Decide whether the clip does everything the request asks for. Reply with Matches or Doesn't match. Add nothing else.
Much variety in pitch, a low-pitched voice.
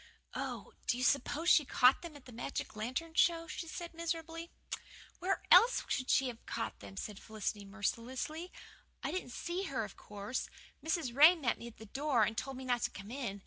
Doesn't match